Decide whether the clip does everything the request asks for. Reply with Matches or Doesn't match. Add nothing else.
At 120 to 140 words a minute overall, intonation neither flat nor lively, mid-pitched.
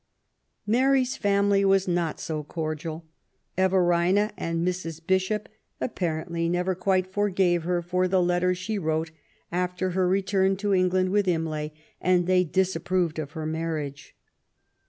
Doesn't match